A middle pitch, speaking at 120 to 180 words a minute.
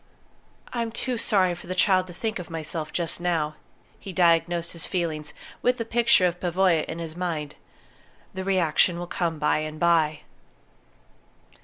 Yes: medium, 175 Hz; average, 160 wpm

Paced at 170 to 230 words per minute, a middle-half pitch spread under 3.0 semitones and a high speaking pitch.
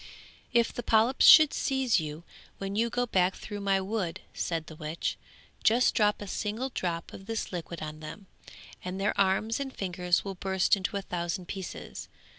No: average, 180 wpm; average, 3.9 semitones; high, 195 Hz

